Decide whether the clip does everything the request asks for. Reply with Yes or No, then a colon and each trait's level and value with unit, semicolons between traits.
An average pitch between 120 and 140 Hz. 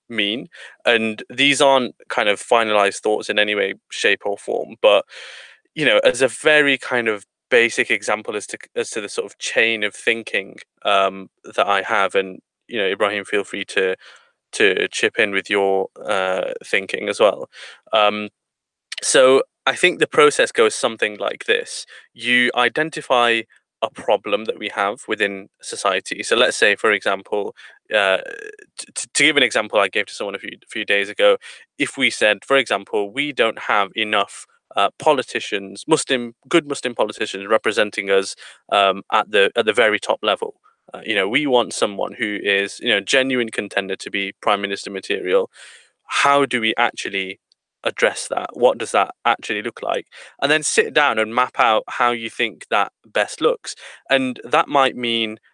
Yes: low, 135 Hz